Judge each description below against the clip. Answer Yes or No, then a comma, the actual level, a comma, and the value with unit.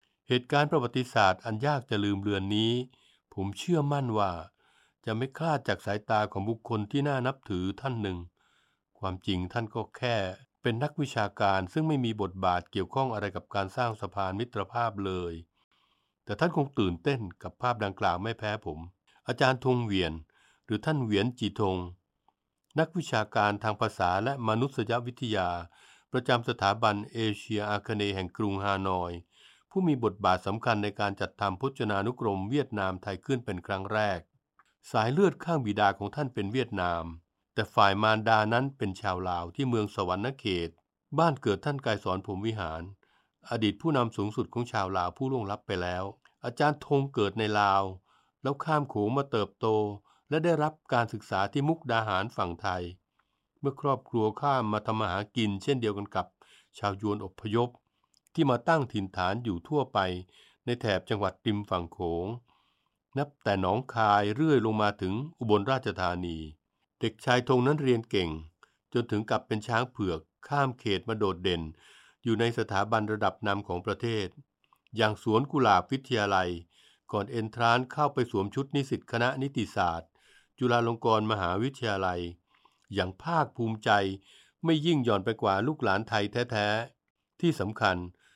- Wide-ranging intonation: No, average, 4.4 semitones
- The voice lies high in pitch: No, low, 110 Hz